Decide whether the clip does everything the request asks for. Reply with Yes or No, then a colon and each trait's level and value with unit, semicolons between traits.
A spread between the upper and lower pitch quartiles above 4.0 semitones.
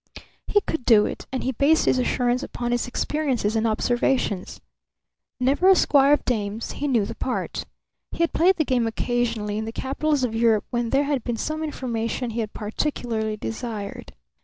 No: average, 3.7 semitones